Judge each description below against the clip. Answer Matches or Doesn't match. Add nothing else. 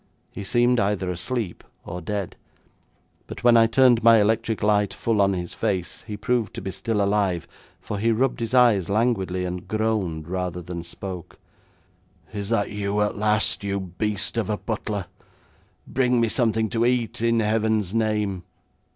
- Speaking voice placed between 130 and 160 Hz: Doesn't match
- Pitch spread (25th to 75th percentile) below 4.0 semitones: Matches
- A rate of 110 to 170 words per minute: Matches